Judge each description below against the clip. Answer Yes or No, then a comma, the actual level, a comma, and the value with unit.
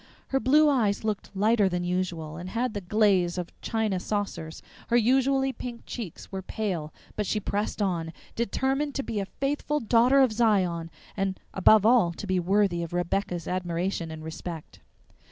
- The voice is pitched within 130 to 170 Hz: No, high, 200 Hz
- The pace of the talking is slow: No, average, 170 wpm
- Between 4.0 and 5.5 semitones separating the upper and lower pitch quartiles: Yes, average, 4.9 semitones